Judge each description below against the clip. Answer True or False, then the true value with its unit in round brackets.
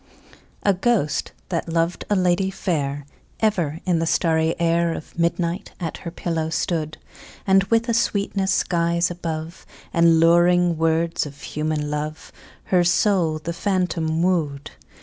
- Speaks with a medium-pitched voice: True (170 Hz)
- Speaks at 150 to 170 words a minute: False (140 wpm)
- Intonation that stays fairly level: True (2.2 semitones)